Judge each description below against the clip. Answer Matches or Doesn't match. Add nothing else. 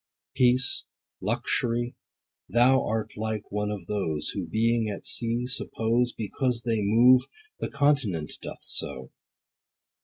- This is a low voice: Matches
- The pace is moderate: Doesn't match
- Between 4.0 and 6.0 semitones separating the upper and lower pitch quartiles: Doesn't match